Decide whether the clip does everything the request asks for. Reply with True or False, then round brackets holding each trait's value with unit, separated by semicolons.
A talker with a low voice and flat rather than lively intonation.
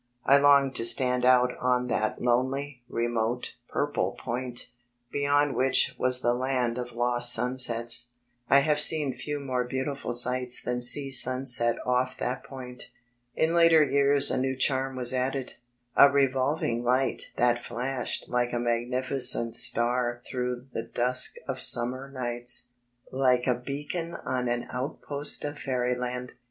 True (125 Hz; 1.8 semitones)